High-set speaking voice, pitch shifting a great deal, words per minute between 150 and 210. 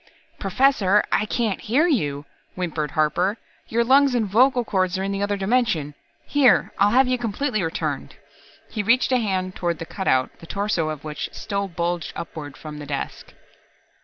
Yes: high, 195 Hz; wide, 6.2 semitones; average, 170 wpm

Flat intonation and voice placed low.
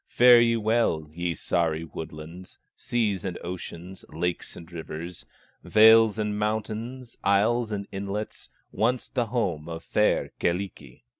No: average, 4.7 semitones; low, 100 Hz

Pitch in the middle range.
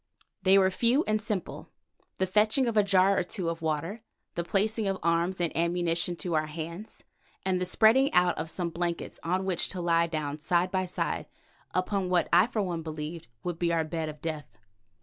Yes: medium, 175 Hz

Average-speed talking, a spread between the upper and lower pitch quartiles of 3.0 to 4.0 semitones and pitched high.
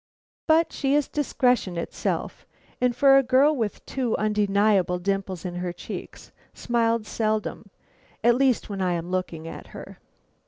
No: average, 150 wpm; wide, 5.6 semitones; high, 215 Hz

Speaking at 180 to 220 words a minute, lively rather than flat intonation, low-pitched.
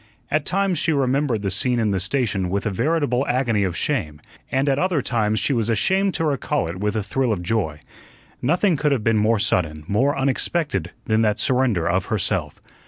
Yes: average, 200 wpm; wide, 6.0 semitones; low, 115 Hz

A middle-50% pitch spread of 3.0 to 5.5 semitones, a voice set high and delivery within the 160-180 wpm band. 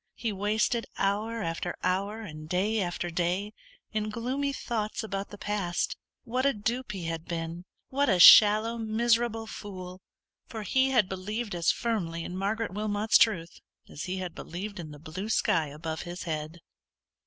Yes: average, 4.2 semitones; high, 205 Hz; average, 165 wpm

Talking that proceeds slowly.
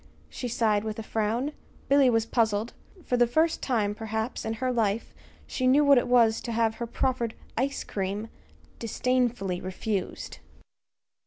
No: average, 155 wpm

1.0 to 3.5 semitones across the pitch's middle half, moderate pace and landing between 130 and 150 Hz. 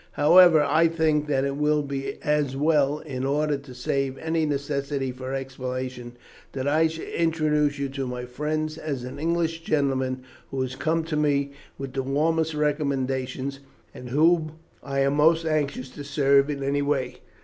Yes: narrow, 2.5 semitones; average, 170 wpm; medium, 140 Hz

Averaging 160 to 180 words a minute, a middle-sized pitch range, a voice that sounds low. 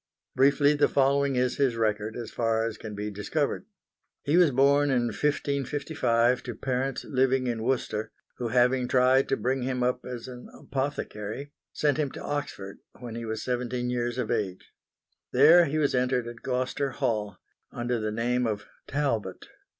Yes: average, 165 wpm; average, 3.1 semitones; low, 125 Hz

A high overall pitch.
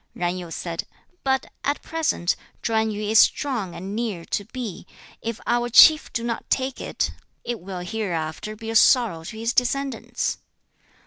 Yes: high, 220 Hz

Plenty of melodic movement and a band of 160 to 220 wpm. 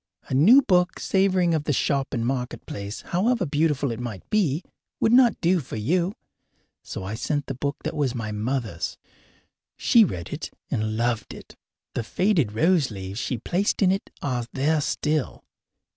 Yes: wide, 7.3 semitones; average, 170 wpm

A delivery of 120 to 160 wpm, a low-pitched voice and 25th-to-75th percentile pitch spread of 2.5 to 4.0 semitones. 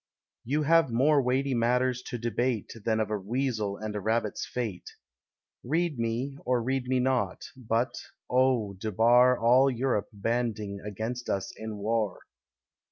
Yes: average, 145 wpm; low, 120 Hz; average, 3.0 semitones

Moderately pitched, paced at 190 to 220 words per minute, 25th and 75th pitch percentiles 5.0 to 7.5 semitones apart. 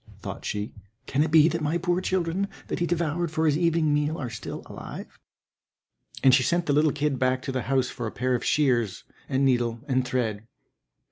No: medium, 145 Hz; fast, 205 wpm; average, 4.3 semitones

